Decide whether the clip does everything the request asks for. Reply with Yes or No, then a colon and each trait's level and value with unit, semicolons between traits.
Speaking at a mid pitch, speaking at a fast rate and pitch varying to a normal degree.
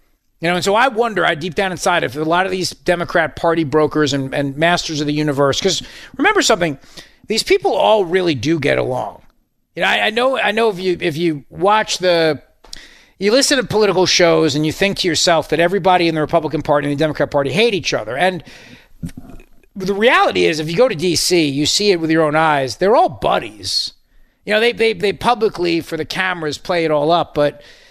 Yes: medium, 170 Hz; fast, 220 wpm; average, 4.3 semitones